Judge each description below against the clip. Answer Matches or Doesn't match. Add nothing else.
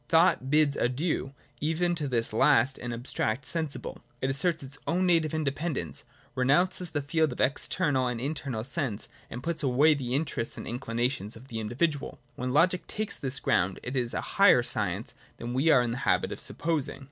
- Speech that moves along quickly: Doesn't match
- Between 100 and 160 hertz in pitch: Matches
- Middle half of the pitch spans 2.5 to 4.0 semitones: Doesn't match